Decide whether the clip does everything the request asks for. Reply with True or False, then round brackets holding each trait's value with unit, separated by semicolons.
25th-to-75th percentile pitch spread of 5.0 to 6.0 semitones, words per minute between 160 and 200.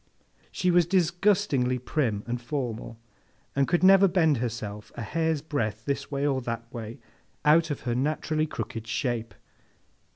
False (5.6 semitones; 150 wpm)